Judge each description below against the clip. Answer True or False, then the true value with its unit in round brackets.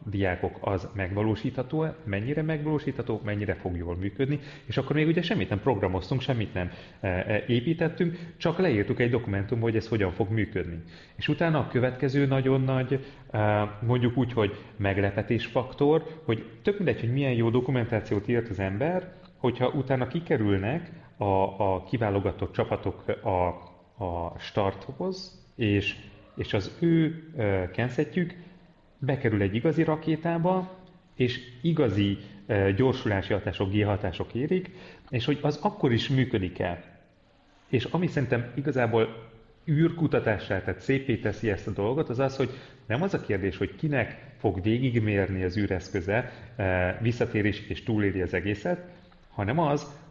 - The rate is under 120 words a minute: False (135 wpm)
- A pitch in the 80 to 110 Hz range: False (120 Hz)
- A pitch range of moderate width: False (6.3 semitones)